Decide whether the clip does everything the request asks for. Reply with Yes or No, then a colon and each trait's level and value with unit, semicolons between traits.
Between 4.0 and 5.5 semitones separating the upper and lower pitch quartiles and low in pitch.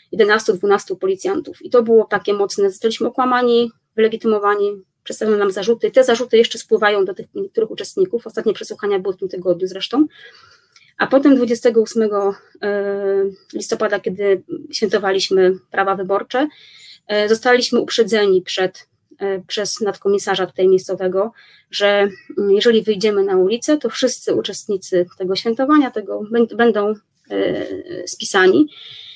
No: average, 4.9 semitones; high, 220 Hz